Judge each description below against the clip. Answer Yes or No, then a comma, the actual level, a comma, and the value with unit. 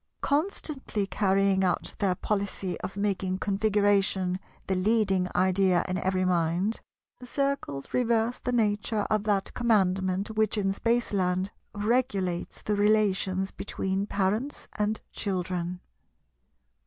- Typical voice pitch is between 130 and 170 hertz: No, high, 200 Hz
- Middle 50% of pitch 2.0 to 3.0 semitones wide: Yes, narrow, 2.5 semitones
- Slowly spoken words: Yes, slow, 115 wpm